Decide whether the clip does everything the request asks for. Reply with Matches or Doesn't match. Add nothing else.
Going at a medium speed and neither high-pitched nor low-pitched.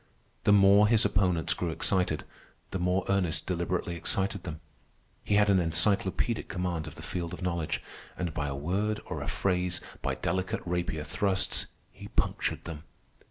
Doesn't match